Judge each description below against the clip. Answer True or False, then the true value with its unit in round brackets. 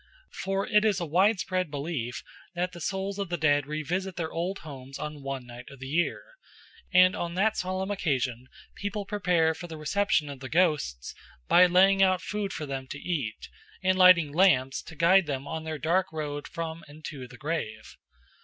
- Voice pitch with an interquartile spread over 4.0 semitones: True (4.6 semitones)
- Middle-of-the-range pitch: True (165 Hz)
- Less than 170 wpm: False (190 wpm)